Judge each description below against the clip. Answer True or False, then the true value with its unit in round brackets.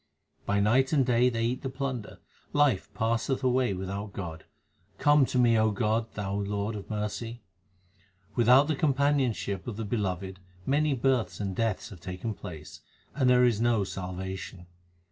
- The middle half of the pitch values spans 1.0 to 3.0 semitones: False (4.2 semitones)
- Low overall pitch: True (115 Hz)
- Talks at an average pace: True (165 wpm)